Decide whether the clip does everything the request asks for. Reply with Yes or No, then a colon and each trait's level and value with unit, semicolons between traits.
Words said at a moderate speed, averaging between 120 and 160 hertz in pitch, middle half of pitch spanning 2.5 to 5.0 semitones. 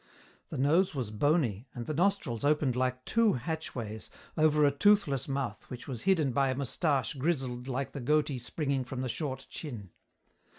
Yes: average, 170 wpm; low, 135 Hz; average, 3.5 semitones